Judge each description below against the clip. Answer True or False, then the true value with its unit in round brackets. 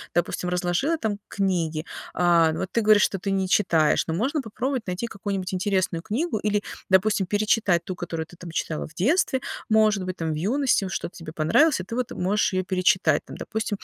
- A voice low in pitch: False (190 Hz)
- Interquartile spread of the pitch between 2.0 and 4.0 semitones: True (3.7 semitones)